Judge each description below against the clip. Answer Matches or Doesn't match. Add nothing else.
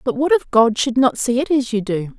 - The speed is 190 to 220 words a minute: Doesn't match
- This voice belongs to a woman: Matches